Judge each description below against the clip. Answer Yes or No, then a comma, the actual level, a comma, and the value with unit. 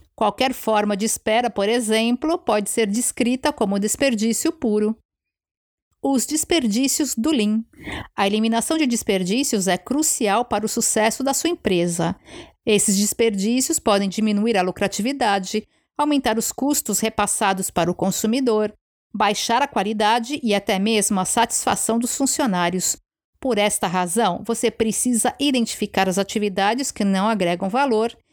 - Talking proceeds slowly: No, average, 135 wpm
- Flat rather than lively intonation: No, average, 3.4 semitones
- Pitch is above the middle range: Yes, high, 225 Hz